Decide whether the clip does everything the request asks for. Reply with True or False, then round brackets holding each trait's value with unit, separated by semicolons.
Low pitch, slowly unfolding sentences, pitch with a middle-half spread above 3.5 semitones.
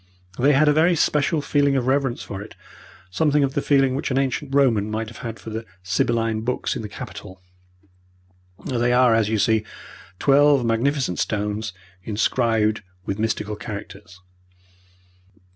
False (120 Hz; 150 wpm; 4.2 semitones)